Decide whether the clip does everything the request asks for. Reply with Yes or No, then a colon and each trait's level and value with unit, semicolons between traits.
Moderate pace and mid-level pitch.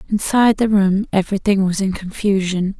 No: average, 150 wpm; high, 195 Hz